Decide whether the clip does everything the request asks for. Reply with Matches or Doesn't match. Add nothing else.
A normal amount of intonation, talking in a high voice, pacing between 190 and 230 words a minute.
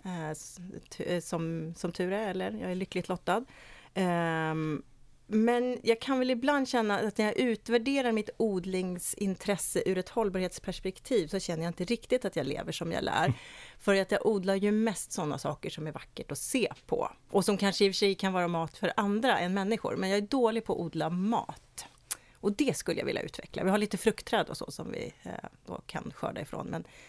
Matches